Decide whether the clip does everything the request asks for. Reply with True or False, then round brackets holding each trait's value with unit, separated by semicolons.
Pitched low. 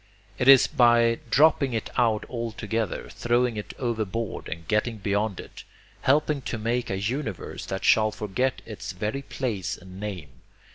True (115 Hz)